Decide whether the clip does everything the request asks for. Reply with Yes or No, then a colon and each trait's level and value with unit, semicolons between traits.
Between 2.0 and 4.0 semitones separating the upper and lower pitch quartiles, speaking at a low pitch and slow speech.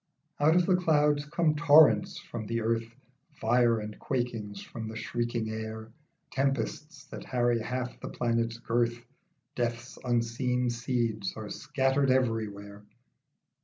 Yes: average, 2.9 semitones; low, 120 Hz; slow, 130 wpm